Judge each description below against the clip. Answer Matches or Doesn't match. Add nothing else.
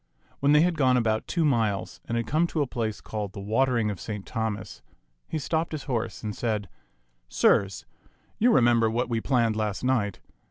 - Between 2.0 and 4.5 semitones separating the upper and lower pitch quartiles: Matches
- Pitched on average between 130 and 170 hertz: Doesn't match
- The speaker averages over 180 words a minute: Matches